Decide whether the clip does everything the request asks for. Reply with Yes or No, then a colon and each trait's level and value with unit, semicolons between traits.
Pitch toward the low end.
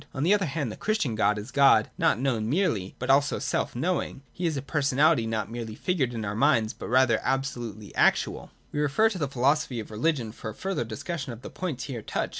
Yes: low, 130 Hz